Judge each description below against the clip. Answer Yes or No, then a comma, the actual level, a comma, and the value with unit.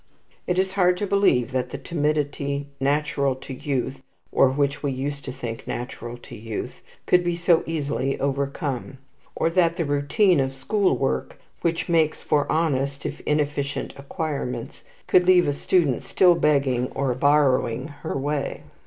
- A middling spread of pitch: Yes, average, 3.6 semitones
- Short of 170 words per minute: Yes, average, 155 wpm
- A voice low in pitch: No, medium, 145 Hz